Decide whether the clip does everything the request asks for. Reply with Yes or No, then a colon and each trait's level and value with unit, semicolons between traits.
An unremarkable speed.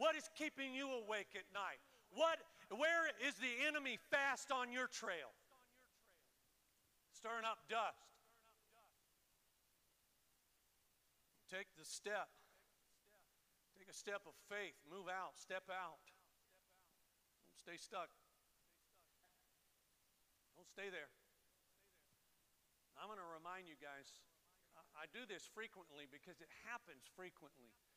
No: slow, 110 wpm